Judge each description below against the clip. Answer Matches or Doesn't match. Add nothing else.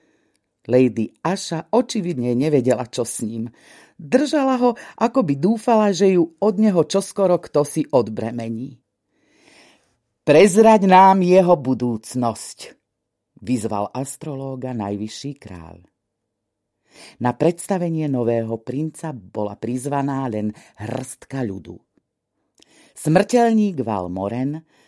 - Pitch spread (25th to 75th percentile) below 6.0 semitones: Doesn't match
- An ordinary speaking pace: Doesn't match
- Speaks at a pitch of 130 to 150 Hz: Matches